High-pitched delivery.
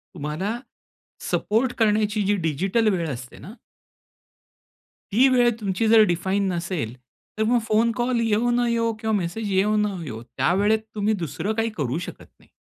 Yes: high, 210 Hz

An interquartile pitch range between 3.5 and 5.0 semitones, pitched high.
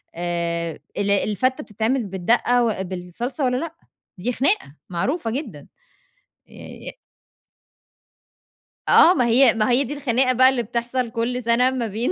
Yes: average, 4.2 semitones; high, 235 Hz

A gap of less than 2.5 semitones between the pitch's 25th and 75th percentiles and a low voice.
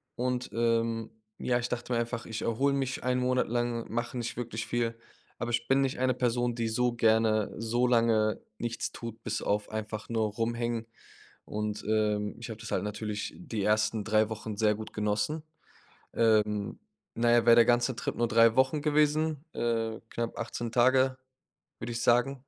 Yes: narrow, 2.0 semitones; low, 115 Hz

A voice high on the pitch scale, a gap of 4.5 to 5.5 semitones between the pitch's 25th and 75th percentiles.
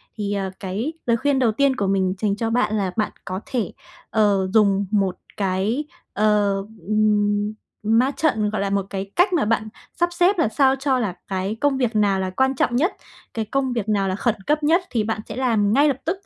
Yes: high, 215 Hz; average, 4.8 semitones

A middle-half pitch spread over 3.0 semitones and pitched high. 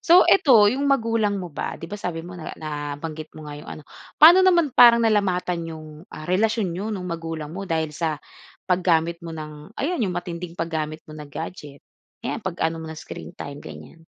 No: average, 4.9 semitones; medium, 170 Hz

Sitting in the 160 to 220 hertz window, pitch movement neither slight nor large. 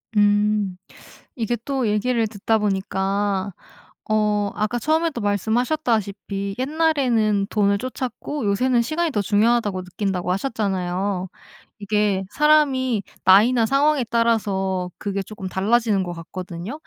Yes: high, 210 Hz; average, 3.7 semitones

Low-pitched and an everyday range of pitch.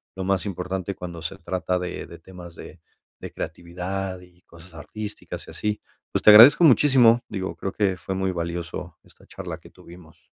No: very low, 95 Hz; narrow, 2.1 semitones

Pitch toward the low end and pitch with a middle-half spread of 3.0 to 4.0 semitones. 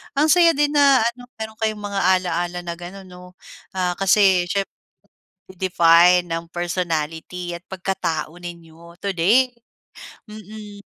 No: medium, 185 Hz; average, 3.5 semitones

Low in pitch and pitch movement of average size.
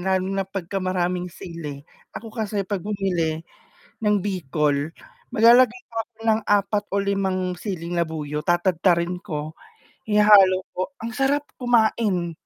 No: medium, 185 Hz; average, 3.4 semitones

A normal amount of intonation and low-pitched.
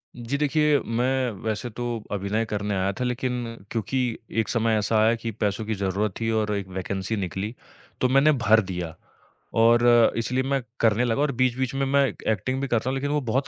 Yes: average, 3.5 semitones; low, 115 Hz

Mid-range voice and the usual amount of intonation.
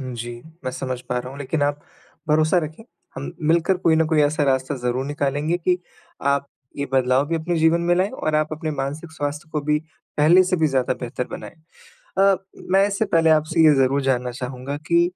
Yes: medium, 150 Hz; average, 3.6 semitones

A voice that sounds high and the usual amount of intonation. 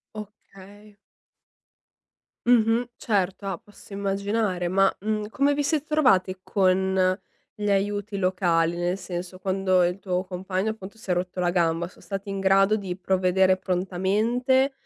No: high, 195 Hz; narrow, 2.3 semitones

